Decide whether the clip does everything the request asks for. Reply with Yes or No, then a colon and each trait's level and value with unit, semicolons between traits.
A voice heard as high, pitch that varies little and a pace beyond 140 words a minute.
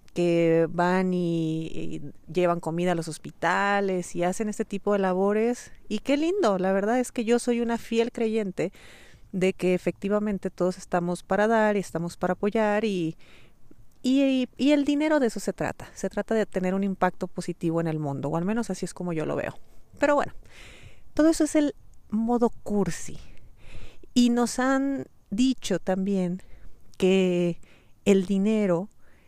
No: high, 195 Hz; average, 4.6 semitones; average, 170 wpm